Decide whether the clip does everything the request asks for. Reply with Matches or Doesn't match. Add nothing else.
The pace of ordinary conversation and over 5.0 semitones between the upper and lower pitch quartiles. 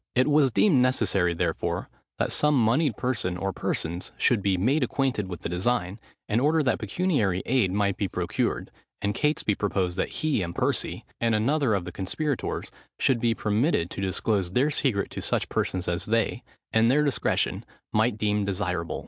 Matches